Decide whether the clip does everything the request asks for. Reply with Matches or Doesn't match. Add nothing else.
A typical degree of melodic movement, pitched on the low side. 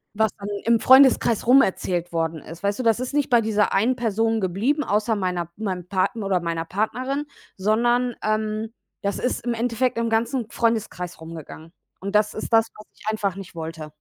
Doesn't match